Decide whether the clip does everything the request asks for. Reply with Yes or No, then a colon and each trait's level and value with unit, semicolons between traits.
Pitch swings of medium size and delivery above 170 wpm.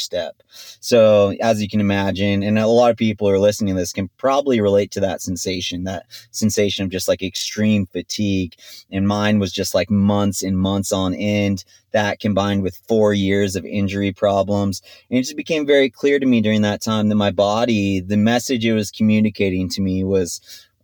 No: narrow, 1.9 semitones; average, 200 wpm